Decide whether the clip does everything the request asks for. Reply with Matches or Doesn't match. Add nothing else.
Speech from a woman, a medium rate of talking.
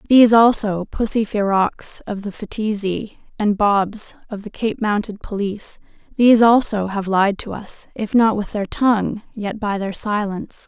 Matches